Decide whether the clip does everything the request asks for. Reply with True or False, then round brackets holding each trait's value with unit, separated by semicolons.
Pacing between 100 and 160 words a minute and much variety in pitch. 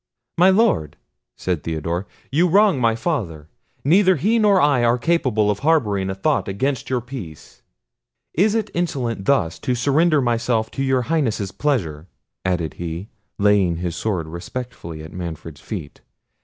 True (150 wpm; 8.9 semitones)